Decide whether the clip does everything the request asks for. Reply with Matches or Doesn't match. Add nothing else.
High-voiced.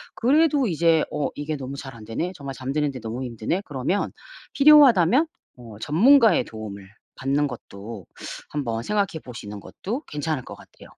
Doesn't match